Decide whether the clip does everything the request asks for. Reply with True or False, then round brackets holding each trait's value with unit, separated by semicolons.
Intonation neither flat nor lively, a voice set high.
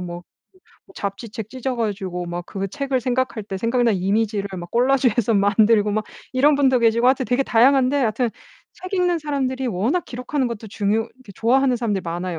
True (4.4 semitones; 230 Hz)